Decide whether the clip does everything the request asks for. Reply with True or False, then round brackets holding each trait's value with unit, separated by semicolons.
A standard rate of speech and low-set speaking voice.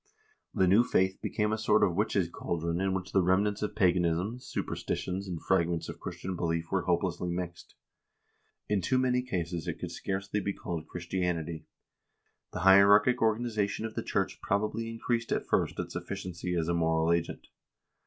True (170 wpm; 95 Hz)